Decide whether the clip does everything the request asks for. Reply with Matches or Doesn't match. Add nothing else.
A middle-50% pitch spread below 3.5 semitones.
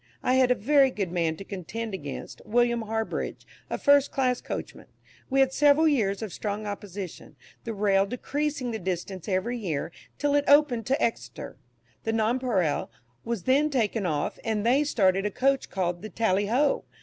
Doesn't match